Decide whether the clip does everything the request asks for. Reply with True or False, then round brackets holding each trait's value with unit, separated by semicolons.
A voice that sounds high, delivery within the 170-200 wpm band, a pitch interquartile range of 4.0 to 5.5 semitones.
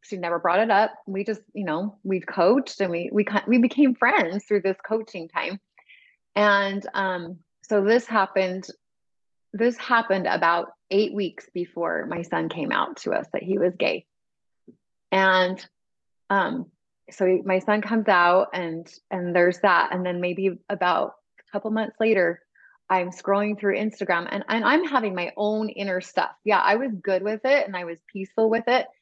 False (200 Hz; 180 wpm; 3.0 semitones)